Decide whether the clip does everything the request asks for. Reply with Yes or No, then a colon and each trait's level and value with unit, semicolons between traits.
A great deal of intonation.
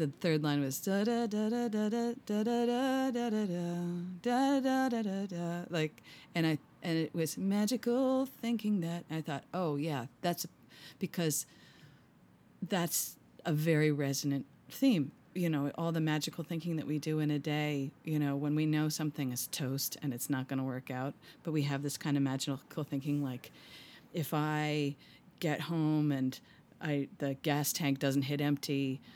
No: average, 4.4 semitones